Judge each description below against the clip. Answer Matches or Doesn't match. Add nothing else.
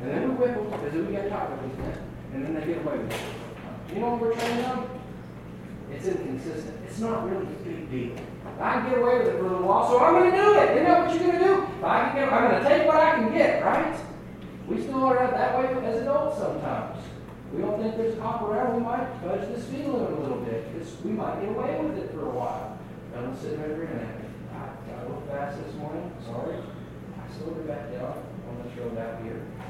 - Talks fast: Matches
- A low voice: Doesn't match